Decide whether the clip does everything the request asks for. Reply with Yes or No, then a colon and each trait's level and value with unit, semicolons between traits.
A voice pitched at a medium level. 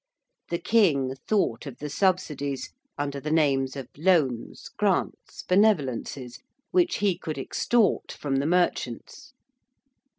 Yes: medium, 150 Hz